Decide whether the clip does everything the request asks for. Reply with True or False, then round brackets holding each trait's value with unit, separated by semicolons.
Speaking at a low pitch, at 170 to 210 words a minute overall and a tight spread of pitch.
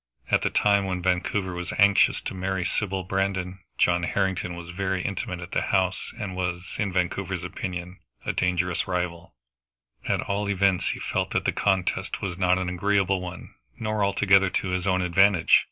True (95 Hz; 175 wpm; 1.6 semitones)